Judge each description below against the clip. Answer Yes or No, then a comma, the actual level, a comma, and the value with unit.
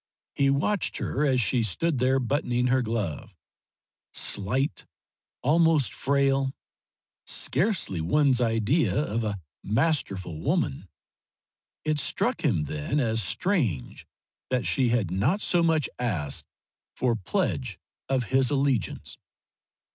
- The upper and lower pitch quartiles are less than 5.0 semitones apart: No, wide, 5.4 semitones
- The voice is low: Yes, low, 130 Hz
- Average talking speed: No, slow, 115 wpm